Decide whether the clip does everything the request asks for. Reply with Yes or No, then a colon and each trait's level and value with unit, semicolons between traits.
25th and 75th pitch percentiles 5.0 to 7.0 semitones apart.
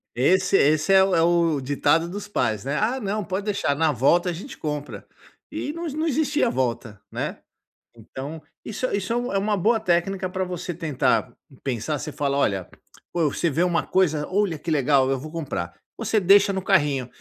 Yes: wide, 5.5 semitones